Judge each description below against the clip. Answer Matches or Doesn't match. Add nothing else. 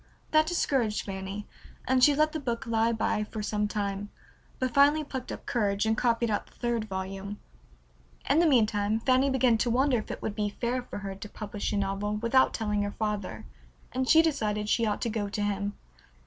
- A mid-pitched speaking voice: Doesn't match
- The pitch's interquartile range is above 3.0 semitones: Matches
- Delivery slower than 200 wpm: Doesn't match